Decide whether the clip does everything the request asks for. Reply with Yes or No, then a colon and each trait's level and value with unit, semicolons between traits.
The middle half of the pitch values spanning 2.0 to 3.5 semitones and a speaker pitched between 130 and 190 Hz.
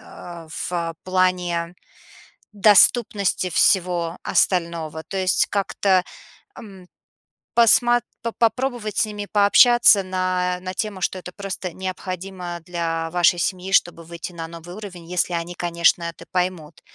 Yes: average, 2.7 semitones; medium, 185 Hz